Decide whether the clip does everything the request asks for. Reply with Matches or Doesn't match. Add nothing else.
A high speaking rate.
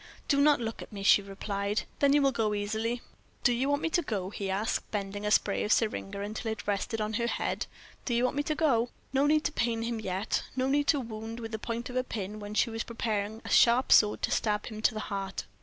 Matches